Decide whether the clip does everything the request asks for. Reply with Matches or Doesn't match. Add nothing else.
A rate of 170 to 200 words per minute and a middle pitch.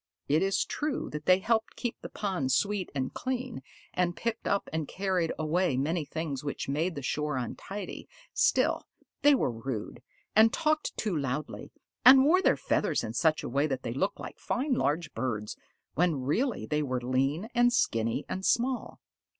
Matches